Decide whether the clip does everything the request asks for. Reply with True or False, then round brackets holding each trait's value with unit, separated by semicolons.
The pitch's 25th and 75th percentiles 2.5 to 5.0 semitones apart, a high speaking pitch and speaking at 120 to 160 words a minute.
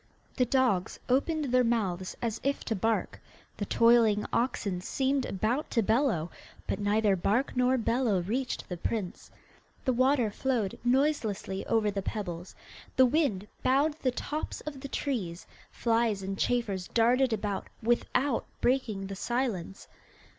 True (4.5 semitones; 230 Hz; 140 wpm)